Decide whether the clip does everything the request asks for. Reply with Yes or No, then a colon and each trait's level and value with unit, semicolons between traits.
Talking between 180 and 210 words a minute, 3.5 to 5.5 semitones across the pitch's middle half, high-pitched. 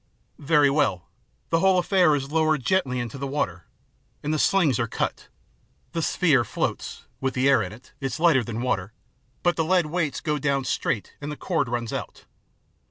No: average, 190 wpm; average, 4.5 semitones; medium, 140 Hz